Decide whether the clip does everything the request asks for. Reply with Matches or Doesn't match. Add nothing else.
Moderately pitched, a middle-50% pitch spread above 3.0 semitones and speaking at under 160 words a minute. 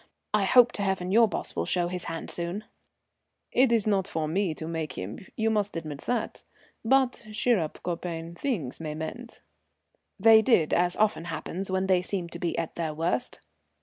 Doesn't match